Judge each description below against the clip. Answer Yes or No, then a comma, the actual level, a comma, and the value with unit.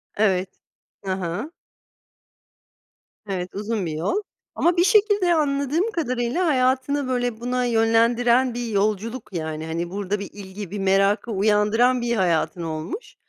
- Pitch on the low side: No, high, 225 Hz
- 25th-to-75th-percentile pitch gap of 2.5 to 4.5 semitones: No, average, 4.9 semitones